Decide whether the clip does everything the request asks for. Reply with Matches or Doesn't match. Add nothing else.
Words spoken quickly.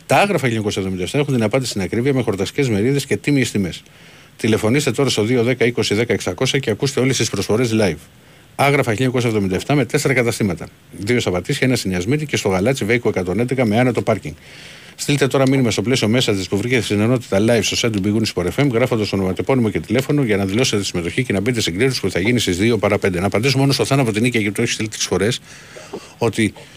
Matches